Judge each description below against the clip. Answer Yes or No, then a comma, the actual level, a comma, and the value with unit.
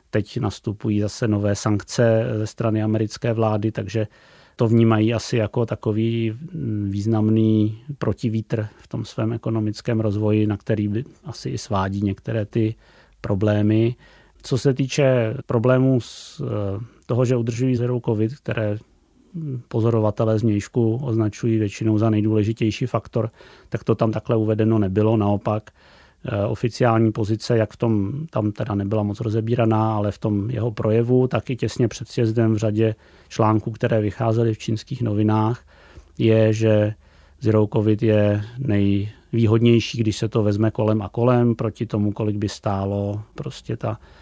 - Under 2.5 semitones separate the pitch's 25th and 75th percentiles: Yes, narrow, 1.7 semitones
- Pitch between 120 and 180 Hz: No, low, 110 Hz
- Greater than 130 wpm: Yes, average, 140 wpm